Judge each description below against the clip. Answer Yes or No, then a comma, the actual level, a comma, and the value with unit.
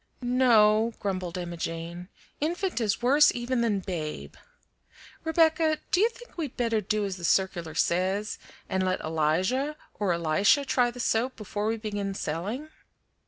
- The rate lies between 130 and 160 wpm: Yes, average, 150 wpm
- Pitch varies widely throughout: Yes, wide, 5.9 semitones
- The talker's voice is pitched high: Yes, high, 210 Hz